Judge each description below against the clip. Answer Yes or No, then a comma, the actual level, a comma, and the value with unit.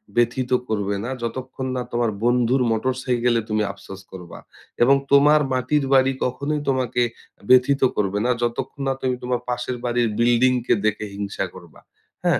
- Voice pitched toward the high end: No, low, 125 Hz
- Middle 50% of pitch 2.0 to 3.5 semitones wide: Yes, narrow, 2.4 semitones